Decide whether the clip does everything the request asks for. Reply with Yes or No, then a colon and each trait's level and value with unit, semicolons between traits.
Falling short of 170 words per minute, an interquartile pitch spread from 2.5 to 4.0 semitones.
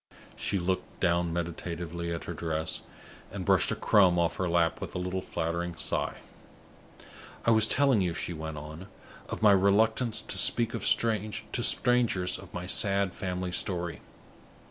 Yes: average, 155 wpm; average, 3.0 semitones